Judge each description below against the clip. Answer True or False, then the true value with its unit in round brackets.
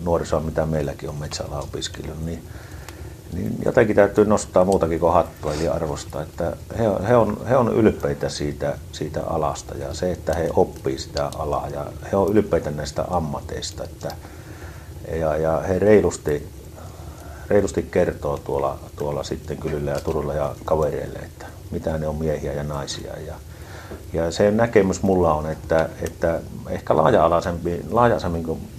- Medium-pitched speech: False (80 Hz)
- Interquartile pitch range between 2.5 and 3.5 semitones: True (2.9 semitones)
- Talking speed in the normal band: True (145 wpm)